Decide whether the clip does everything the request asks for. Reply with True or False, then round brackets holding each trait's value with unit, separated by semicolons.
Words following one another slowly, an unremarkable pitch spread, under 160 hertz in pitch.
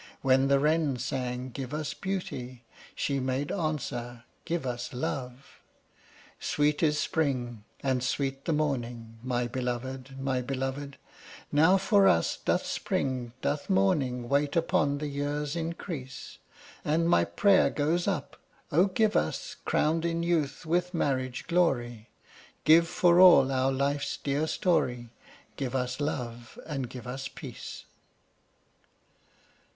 True (130 wpm; 3.9 semitones; 140 Hz)